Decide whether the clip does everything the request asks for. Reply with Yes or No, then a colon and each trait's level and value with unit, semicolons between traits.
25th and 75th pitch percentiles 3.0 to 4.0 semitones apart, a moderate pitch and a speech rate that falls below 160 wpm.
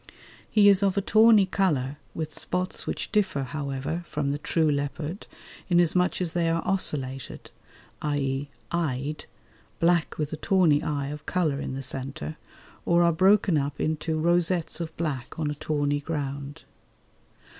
Yes: average, 3.7 semitones; medium, 155 Hz; average, 150 wpm